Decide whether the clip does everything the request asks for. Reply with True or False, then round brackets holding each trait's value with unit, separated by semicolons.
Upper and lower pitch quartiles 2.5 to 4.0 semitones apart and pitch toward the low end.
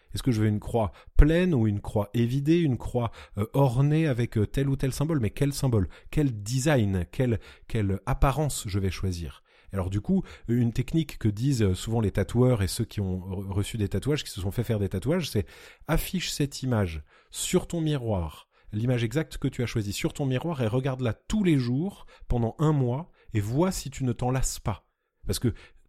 False (5.5 semitones; 120 Hz)